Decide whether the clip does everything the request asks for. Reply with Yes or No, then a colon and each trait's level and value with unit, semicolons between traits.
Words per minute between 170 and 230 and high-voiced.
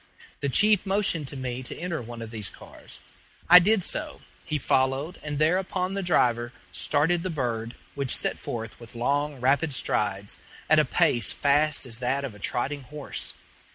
No: average, 175 wpm; medium, 140 Hz